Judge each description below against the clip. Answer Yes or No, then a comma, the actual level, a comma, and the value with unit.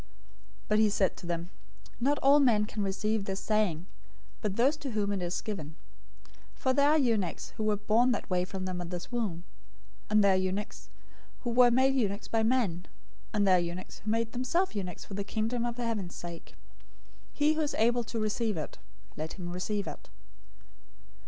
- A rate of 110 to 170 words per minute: No, average, 195 wpm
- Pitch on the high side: Yes, high, 210 Hz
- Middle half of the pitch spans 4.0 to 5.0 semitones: Yes, average, 4.4 semitones